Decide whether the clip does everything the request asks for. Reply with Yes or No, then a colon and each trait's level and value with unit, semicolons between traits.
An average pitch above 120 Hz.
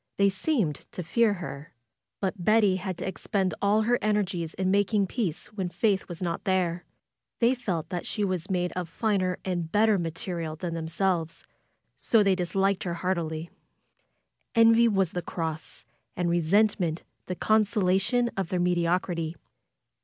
Yes: medium, 185 Hz